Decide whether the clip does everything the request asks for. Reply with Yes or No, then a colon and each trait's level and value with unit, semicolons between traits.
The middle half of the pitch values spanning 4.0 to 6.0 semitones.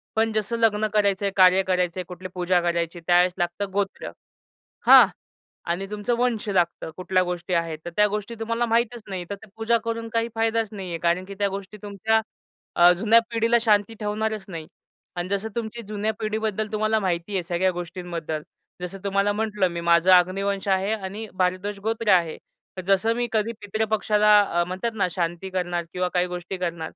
No: average, 3.5 semitones